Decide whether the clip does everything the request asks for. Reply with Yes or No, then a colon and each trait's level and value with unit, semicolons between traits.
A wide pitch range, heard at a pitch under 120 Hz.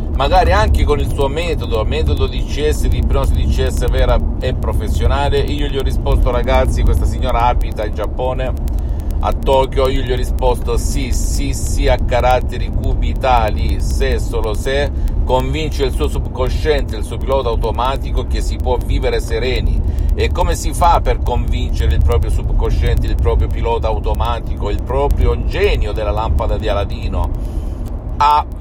Yes: wide, 5.9 semitones; very low, 80 Hz